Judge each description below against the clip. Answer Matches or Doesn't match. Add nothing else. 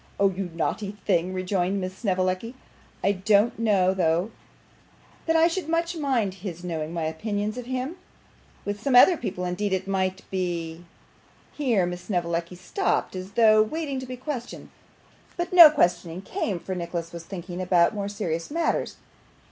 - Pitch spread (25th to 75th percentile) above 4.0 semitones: Matches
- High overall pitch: Matches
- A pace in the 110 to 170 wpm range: Matches